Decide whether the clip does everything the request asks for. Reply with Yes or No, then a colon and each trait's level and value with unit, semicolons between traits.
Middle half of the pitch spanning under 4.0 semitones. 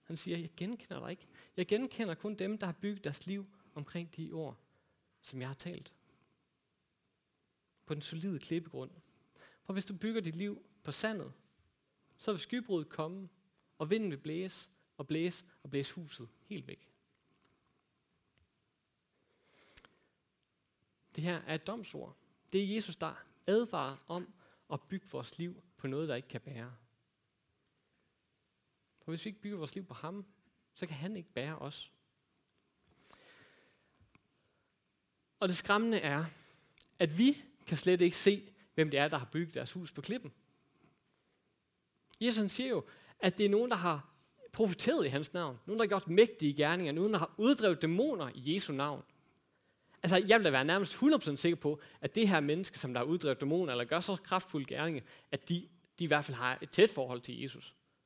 No: average, 4.6 semitones